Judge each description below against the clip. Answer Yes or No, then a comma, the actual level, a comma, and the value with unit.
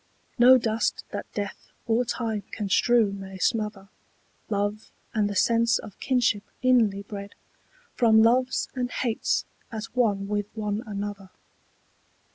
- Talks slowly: Yes, slow, 130 wpm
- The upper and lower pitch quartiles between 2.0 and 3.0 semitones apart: Yes, narrow, 2.4 semitones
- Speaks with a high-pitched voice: Yes, high, 215 Hz